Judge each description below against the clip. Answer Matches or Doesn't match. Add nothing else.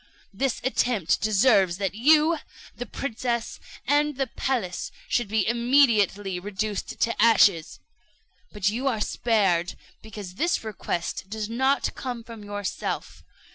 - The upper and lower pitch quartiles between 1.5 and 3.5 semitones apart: Doesn't match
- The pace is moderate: Doesn't match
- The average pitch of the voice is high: Matches